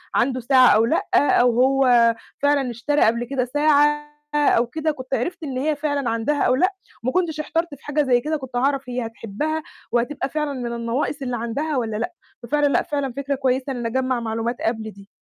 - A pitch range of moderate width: Yes, average, 3.6 semitones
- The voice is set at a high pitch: Yes, very high, 265 Hz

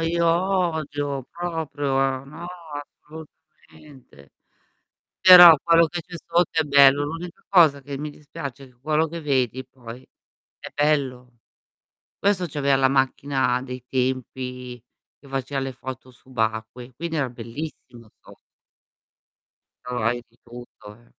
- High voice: No, medium, 140 Hz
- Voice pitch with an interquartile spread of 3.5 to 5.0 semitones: Yes, average, 4.0 semitones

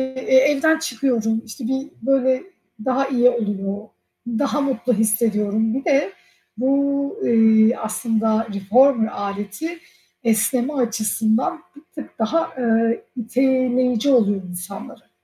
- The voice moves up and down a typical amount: Yes, average, 3.6 semitones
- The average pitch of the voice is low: No, high, 240 Hz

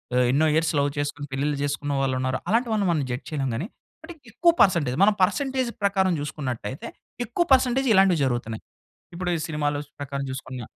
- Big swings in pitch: Yes, wide, 6.5 semitones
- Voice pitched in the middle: Yes, medium, 150 Hz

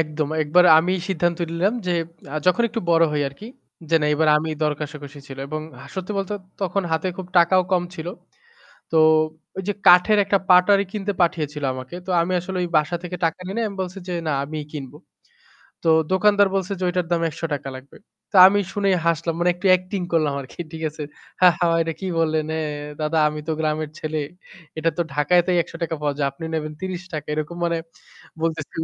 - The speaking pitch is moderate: Yes, medium, 165 Hz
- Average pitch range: Yes, average, 3.3 semitones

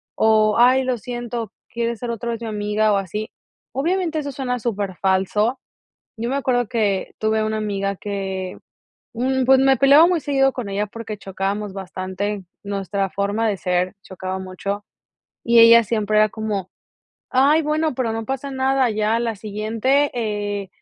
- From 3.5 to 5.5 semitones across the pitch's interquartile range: Yes, average, 3.9 semitones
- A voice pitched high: Yes, high, 220 Hz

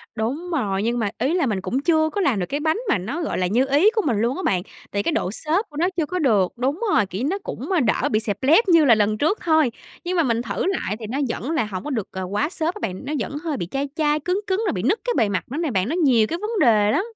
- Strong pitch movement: Yes, wide, 7.4 semitones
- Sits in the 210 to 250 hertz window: No, very high, 275 Hz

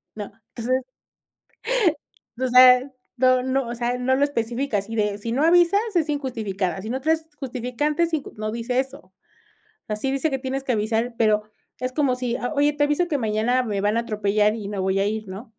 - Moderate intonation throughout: Yes, average, 4.1 semitones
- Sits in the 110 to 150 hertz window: No, high, 245 Hz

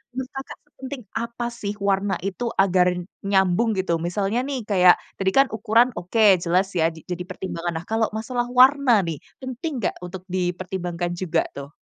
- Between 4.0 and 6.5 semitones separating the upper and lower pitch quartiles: Yes, average, 5.1 semitones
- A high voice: Yes, high, 195 Hz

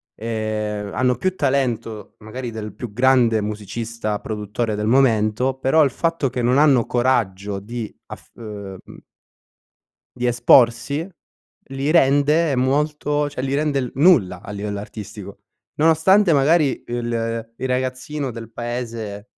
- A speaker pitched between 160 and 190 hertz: No, low, 120 Hz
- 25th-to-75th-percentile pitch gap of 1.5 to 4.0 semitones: No, average, 4.4 semitones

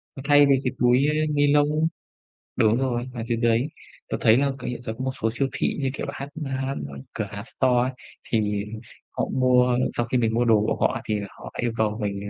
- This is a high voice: No, low, 125 Hz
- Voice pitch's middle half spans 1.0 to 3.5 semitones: Yes, average, 3.2 semitones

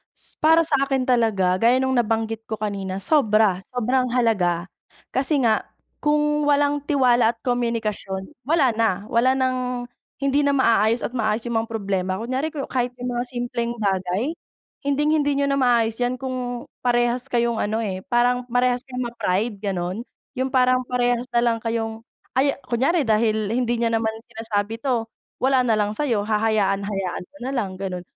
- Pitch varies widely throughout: No, average, 2.9 semitones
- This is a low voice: No, high, 235 Hz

